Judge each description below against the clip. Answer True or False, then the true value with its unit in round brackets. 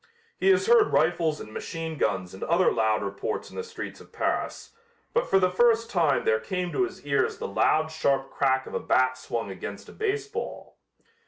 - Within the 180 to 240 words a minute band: True (195 wpm)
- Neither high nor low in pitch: True (160 Hz)